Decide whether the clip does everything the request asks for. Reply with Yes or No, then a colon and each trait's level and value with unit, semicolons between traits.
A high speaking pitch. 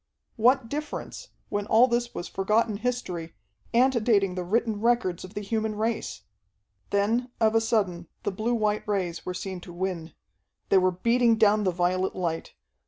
Yes: high, 210 Hz